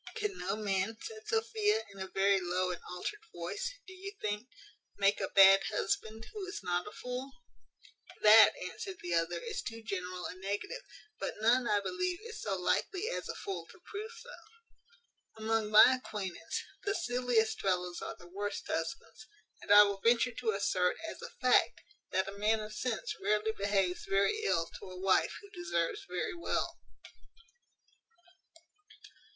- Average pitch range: No, wide, 6.2 semitones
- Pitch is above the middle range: Yes, high, 215 Hz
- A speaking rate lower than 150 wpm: No, average, 165 wpm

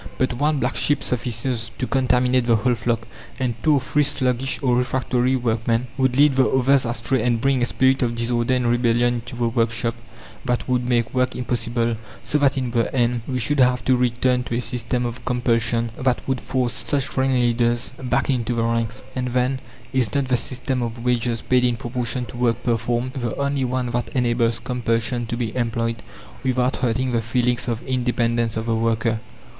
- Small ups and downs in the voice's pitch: Yes, narrow, 1.6 semitones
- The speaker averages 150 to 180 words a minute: No, average, 195 wpm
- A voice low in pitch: Yes, low, 125 Hz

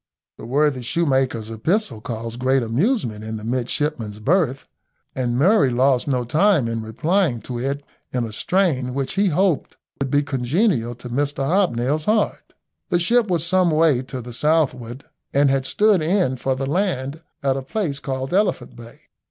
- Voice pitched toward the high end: No, low, 135 Hz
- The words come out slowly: No, average, 170 wpm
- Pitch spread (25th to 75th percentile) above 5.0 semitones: Yes, wide, 5.5 semitones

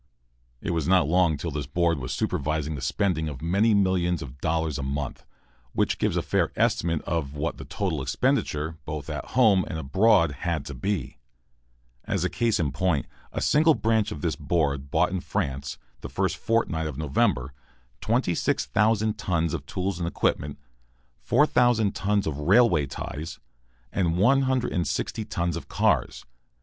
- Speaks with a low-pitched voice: Yes, very low, 85 Hz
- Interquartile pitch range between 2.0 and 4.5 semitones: No, average, 5.1 semitones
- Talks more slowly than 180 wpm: Yes, average, 160 wpm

